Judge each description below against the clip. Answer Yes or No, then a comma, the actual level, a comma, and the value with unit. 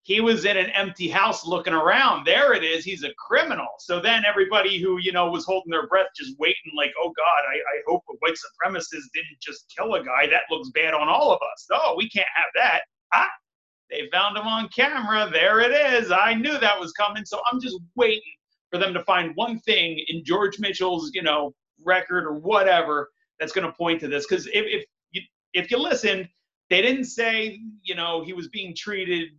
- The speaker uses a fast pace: Yes, fast, 215 wpm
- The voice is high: Yes, high, 195 Hz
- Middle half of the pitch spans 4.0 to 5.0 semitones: Yes, average, 4.4 semitones